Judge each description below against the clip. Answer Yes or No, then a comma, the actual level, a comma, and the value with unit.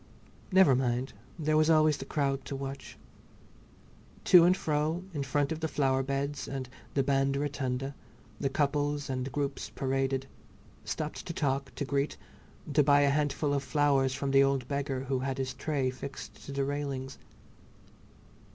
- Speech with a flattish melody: Yes, narrow, 1.5 semitones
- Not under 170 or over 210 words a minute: No, average, 160 wpm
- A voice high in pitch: No, medium, 140 Hz